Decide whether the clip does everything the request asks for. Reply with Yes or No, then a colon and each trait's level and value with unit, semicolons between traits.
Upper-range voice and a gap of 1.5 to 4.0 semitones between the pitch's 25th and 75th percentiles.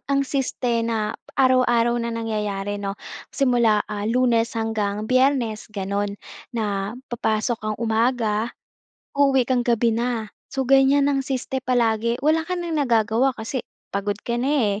Yes: high, 235 Hz; average, 3.2 semitones